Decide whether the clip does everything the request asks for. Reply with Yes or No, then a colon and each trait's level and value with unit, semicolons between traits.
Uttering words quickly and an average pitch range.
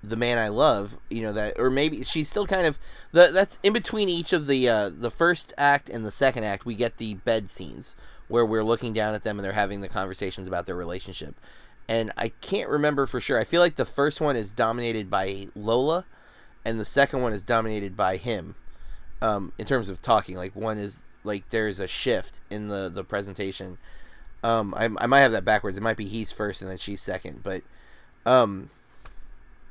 Yes: fast, 210 wpm; average, 4.5 semitones